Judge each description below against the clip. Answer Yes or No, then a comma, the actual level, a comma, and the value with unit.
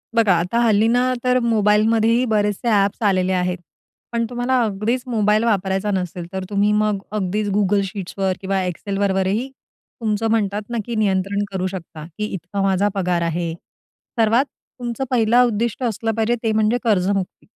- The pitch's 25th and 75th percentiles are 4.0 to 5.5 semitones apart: No, average, 3.0 semitones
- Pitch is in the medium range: No, high, 210 Hz